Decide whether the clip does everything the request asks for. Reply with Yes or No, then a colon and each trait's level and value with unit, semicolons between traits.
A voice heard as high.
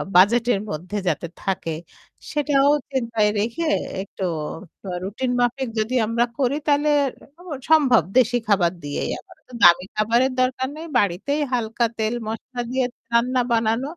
Yes: high, 235 Hz